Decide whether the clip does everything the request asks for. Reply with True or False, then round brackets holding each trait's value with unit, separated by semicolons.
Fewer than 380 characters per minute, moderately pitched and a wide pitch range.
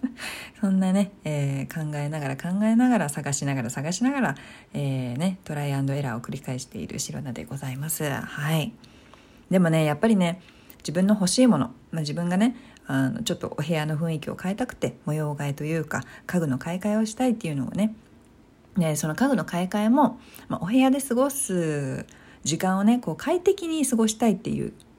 False (385 characters per minute; 175 Hz; 7.0 semitones)